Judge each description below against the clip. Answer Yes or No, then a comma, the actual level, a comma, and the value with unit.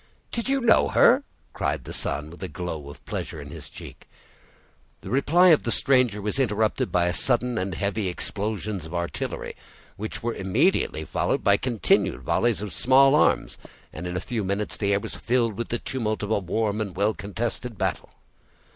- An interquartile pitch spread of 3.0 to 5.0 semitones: Yes, average, 4.5 semitones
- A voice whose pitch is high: No, low, 105 Hz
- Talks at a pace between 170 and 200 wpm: Yes, average, 185 wpm